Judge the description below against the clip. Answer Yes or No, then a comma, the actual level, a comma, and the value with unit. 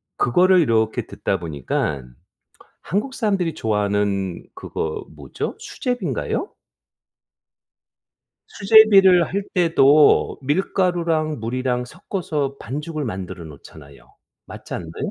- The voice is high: No, medium, 140 Hz